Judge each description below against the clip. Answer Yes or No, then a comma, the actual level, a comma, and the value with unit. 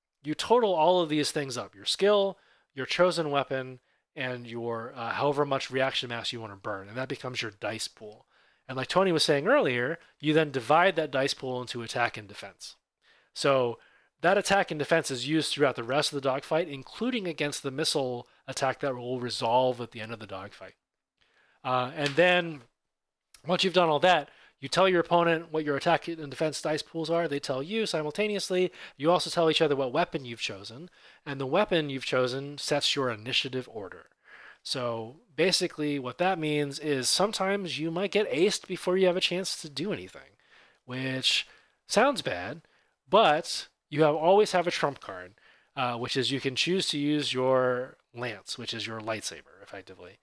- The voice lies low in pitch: No, medium, 145 Hz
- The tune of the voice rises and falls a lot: No, average, 4.7 semitones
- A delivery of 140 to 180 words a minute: No, average, 190 wpm